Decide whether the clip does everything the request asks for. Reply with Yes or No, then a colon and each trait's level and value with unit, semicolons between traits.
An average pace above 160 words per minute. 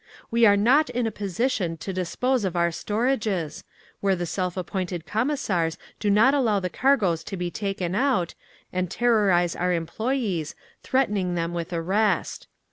No: average, 155 wpm